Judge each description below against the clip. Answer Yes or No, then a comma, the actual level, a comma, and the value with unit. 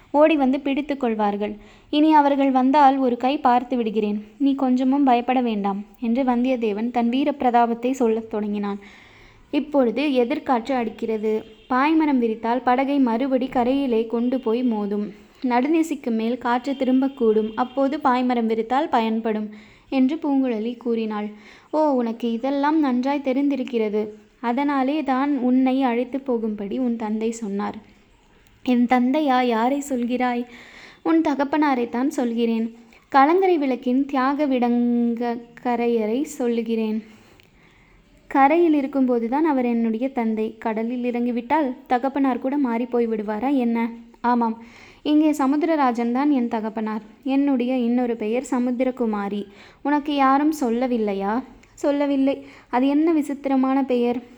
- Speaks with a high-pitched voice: Yes, very high, 250 Hz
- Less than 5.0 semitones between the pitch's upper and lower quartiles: Yes, average, 2.9 semitones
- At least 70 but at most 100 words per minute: No, average, 110 wpm